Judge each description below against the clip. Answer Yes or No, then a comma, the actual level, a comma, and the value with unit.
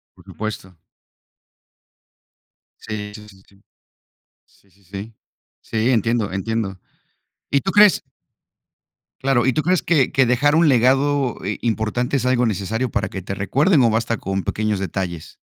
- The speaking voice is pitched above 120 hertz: No, low, 115 Hz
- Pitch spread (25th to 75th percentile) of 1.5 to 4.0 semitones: No, average, 4.7 semitones